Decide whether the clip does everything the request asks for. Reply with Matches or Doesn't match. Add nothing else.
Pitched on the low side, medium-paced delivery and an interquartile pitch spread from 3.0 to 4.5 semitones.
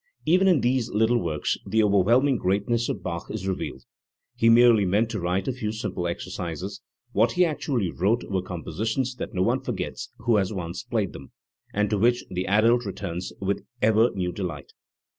Matches